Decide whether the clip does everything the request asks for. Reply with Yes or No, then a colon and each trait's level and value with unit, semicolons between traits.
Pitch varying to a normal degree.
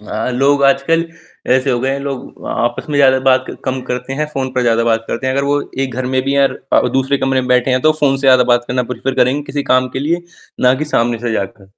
No: narrow, 1.8 semitones